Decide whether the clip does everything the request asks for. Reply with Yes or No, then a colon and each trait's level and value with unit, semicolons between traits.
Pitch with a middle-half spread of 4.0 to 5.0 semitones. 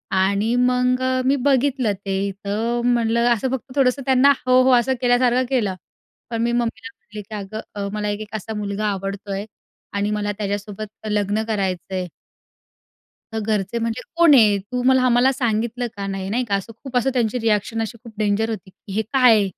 No: average, 3.5 semitones